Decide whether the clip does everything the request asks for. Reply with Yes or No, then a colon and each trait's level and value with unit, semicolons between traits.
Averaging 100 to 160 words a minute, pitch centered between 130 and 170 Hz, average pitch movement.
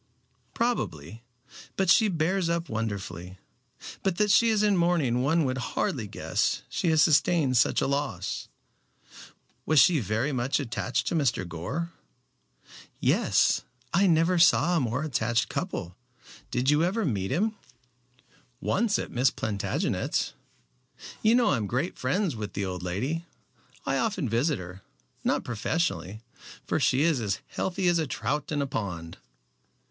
No: average, 150 wpm; medium, 140 Hz; wide, 7.5 semitones